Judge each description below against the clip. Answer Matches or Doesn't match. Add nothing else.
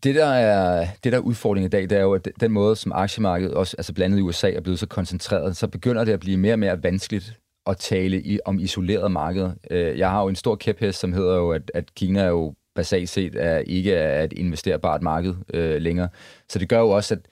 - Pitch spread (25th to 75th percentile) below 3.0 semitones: Matches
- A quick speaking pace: Matches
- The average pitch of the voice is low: Matches